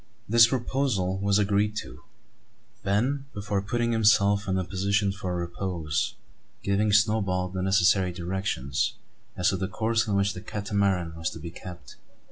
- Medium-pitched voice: No, low, 100 Hz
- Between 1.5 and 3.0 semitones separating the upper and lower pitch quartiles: Yes, narrow, 2.5 semitones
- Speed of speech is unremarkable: Yes, average, 150 wpm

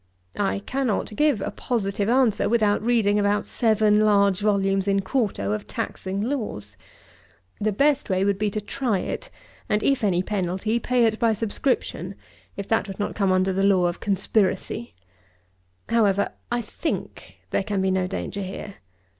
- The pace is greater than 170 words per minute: No, average, 165 wpm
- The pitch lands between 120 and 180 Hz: No, high, 205 Hz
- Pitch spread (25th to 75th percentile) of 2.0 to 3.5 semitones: Yes, narrow, 2.6 semitones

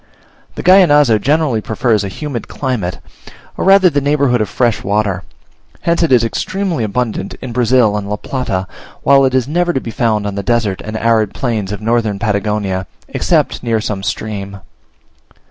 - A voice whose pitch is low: Yes, low, 115 Hz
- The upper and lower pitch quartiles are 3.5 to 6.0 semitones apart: Yes, average, 4.3 semitones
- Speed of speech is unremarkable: Yes, average, 160 wpm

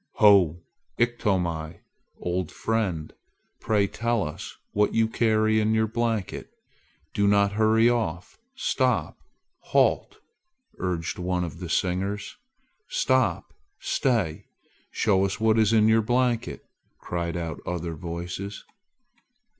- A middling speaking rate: No, slow, 115 wpm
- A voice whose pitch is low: Yes, low, 100 Hz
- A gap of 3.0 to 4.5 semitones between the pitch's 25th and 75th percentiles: Yes, average, 4.0 semitones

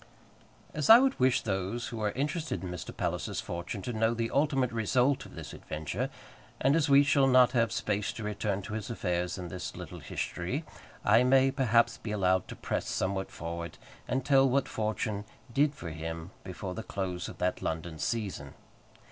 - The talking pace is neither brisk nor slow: Yes, average, 185 wpm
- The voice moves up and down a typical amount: No, wide, 6.2 semitones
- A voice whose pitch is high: No, low, 110 Hz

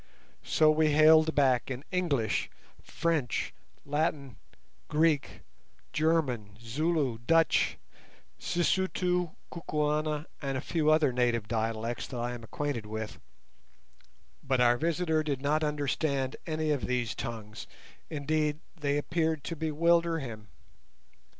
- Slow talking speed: Yes, slow, 115 wpm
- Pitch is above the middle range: No, medium, 150 Hz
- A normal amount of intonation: Yes, average, 4.3 semitones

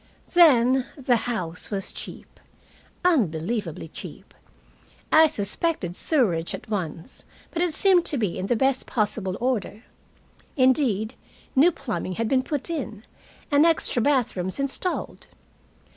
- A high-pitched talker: Yes, high, 245 Hz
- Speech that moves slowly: Yes, slow, 125 wpm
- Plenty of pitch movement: Yes, wide, 6.4 semitones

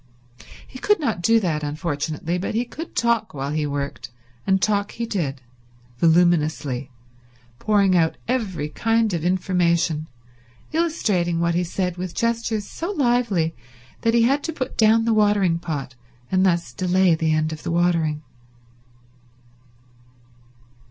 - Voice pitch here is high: No, medium, 180 Hz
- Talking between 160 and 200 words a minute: No, average, 140 wpm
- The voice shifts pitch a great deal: Yes, wide, 5.9 semitones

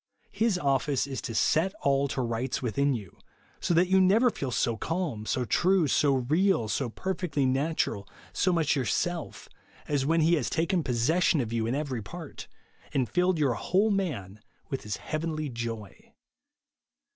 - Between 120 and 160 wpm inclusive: No, average, 175 wpm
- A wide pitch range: Yes, wide, 6.2 semitones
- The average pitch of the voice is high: No, medium, 140 Hz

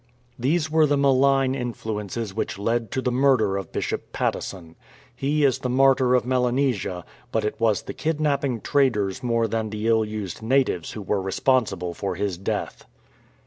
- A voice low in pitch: Yes, low, 115 Hz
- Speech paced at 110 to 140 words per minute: No, average, 165 wpm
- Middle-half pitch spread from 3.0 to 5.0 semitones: Yes, average, 4.5 semitones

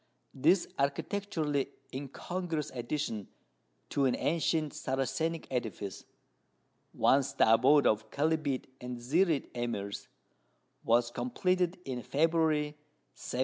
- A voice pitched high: No, medium, 140 Hz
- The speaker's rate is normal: No, slow, 100 wpm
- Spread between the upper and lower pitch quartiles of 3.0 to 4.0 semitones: No, average, 4.8 semitones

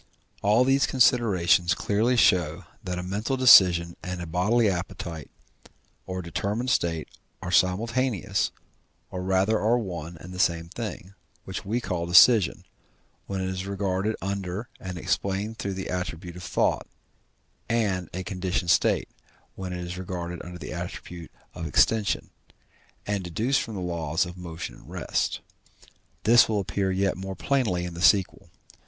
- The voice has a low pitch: Yes, very low, 95 Hz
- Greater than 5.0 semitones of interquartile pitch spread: No, average, 3.1 semitones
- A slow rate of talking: No, average, 150 wpm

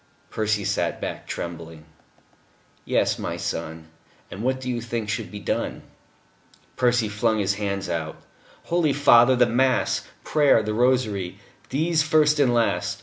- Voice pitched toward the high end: No, low, 115 Hz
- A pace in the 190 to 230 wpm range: No, average, 145 wpm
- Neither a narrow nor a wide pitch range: Yes, average, 4.4 semitones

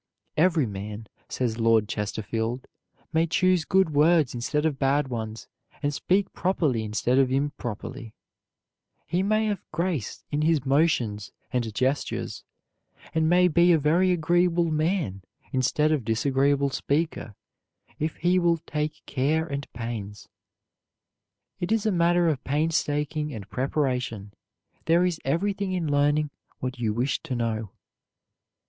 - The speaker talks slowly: Yes, slow, 130 wpm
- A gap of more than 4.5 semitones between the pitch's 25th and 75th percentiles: Yes, wide, 5.6 semitones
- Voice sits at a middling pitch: Yes, medium, 145 Hz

